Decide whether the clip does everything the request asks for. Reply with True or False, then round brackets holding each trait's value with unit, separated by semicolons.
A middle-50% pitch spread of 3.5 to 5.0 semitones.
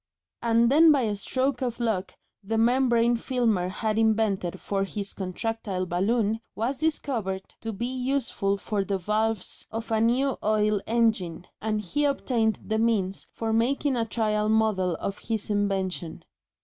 False (3.0 semitones)